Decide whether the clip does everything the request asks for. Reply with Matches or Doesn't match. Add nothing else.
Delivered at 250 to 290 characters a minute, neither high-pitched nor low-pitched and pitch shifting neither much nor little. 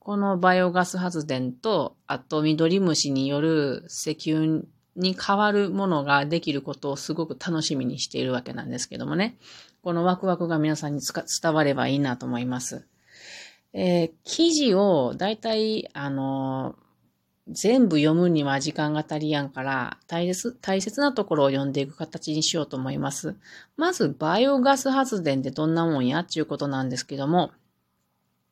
Doesn't match